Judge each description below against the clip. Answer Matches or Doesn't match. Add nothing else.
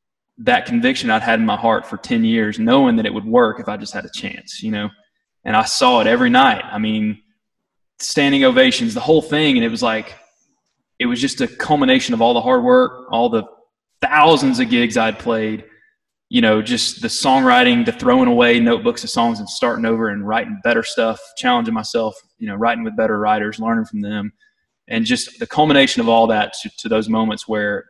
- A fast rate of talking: Matches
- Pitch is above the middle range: Matches